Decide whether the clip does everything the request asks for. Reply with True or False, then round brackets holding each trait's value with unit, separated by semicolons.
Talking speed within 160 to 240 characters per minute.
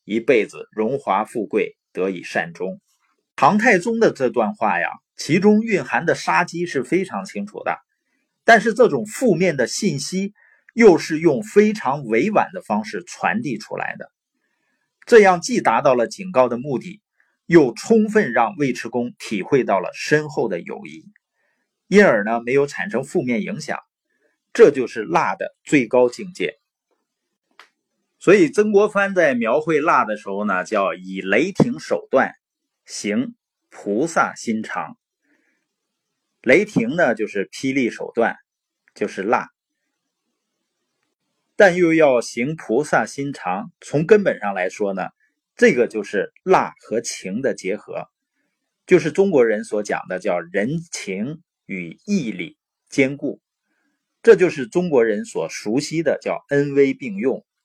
True (205 characters per minute)